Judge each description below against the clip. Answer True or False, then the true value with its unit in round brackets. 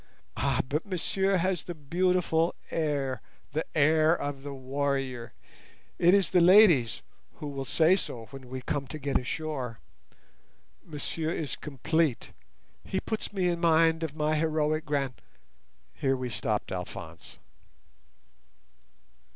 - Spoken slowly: True (125 wpm)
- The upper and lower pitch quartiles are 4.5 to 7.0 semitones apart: False (3.6 semitones)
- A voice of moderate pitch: True (150 Hz)